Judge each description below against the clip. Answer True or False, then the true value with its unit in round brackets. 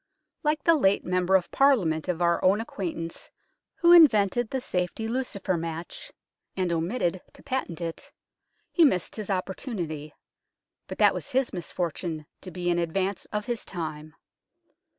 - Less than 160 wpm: True (150 wpm)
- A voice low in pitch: False (185 Hz)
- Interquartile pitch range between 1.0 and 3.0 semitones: False (5.3 semitones)